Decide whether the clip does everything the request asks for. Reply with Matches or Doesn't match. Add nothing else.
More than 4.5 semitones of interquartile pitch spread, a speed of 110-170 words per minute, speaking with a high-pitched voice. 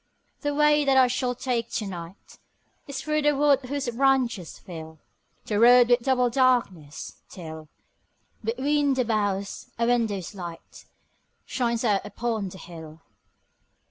Matches